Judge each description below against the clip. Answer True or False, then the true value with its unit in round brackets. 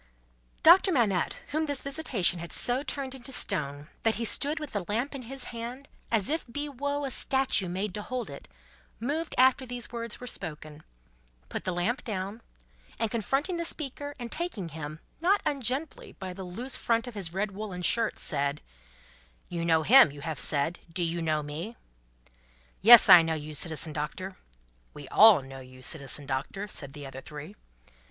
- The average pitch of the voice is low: False (210 Hz)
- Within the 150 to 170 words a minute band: False (180 wpm)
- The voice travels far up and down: True (8.3 semitones)